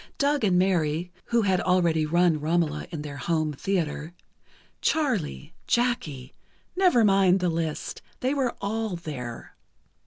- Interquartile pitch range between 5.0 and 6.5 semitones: Yes, wide, 5.4 semitones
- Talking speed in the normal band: No, slow, 130 wpm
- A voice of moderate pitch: Yes, medium, 175 Hz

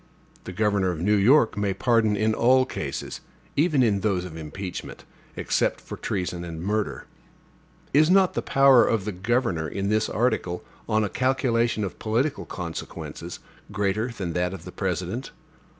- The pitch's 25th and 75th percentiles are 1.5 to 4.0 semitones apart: No, average, 4.7 semitones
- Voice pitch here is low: Yes, low, 105 Hz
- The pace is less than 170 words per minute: Yes, average, 160 wpm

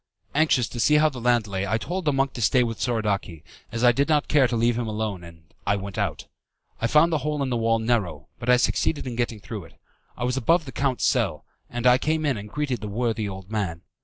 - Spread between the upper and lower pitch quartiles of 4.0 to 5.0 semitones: Yes, average, 4.3 semitones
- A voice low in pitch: Yes, low, 120 Hz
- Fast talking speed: Yes, fast, 250 wpm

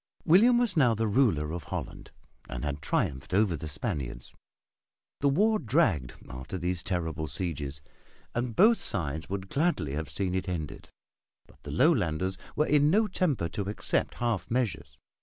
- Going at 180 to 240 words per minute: No, average, 160 wpm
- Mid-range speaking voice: No, very low, 95 Hz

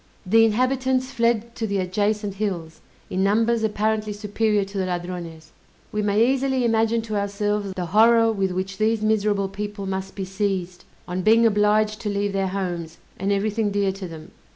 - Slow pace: No, average, 175 wpm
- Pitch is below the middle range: No, high, 205 Hz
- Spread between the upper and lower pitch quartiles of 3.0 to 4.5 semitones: No, narrow, 2.4 semitones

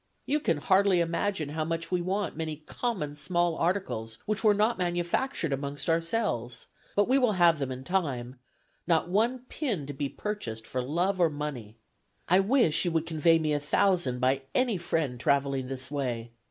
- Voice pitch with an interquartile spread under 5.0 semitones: No, wide, 5.5 semitones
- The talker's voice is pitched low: No, medium, 165 Hz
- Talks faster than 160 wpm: Yes, average, 180 wpm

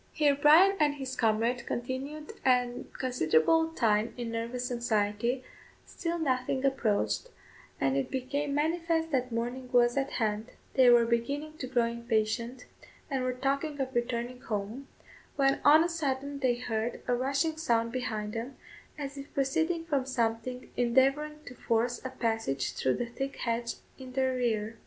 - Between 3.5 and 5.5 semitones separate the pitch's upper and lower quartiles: No, average, 3.1 semitones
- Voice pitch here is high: Yes, very high, 255 Hz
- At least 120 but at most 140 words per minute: No, average, 155 wpm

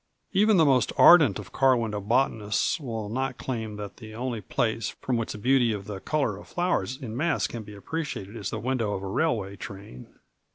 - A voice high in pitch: No, low, 115 Hz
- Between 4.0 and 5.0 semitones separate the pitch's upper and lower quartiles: Yes, average, 4.4 semitones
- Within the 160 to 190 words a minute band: No, fast, 205 wpm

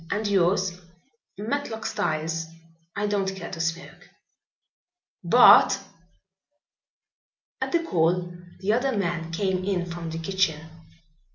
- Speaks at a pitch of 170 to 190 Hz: Yes, medium, 185 Hz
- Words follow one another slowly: Yes, slow, 110 wpm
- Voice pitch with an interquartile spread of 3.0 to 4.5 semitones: Yes, average, 3.5 semitones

